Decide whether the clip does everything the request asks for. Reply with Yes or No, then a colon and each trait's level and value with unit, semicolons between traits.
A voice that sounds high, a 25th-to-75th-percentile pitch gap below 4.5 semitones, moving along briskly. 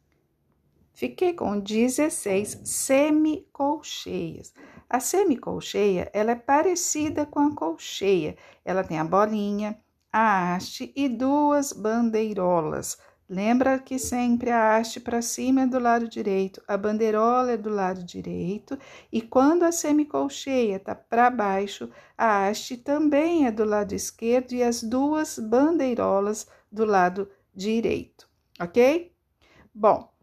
No: high, 235 Hz; wide, 5.4 semitones; fast, 120 wpm